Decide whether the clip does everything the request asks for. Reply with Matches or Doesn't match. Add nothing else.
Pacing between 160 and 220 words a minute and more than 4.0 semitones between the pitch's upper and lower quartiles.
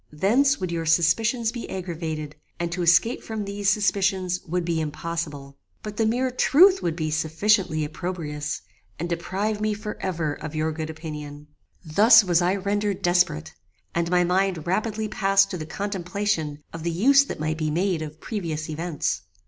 Matches